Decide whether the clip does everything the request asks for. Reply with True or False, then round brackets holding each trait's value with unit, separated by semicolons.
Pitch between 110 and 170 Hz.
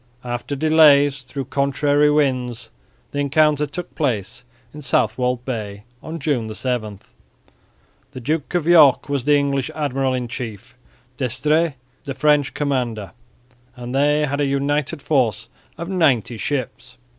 True (140 Hz)